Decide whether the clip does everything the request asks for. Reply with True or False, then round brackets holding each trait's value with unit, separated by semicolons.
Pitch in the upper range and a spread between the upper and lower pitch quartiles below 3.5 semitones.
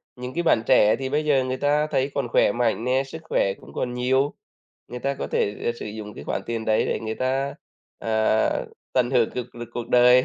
False (125 Hz; 2.6 semitones)